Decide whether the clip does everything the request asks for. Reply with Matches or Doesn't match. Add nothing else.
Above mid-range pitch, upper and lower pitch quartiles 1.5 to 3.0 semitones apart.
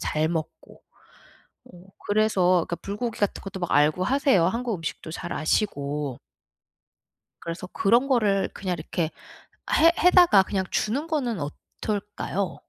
Doesn't match